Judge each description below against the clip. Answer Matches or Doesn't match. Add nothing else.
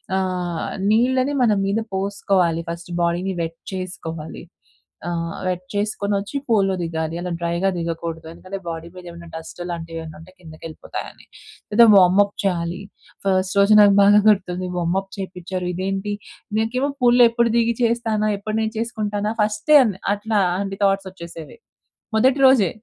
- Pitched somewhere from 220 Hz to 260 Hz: Doesn't match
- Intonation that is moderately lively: Matches